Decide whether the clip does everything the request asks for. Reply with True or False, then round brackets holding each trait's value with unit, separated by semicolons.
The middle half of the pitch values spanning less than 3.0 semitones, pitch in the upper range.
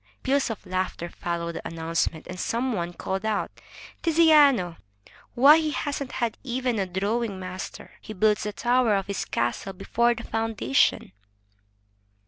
False (5.3 semitones; 215 Hz)